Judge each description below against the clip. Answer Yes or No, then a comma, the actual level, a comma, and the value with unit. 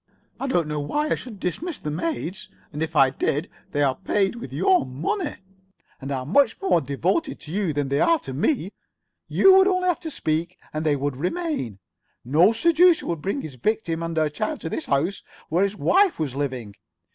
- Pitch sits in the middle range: Yes, medium, 170 Hz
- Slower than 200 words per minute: No, fast, 205 wpm